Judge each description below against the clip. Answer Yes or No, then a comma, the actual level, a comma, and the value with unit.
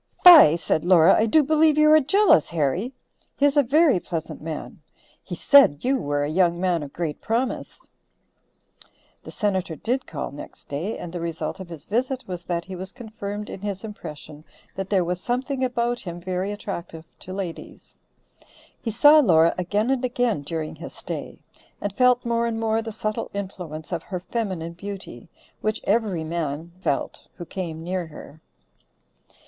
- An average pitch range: No, wide, 5.9 semitones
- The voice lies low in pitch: No, high, 190 Hz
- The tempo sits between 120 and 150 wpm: No, average, 175 wpm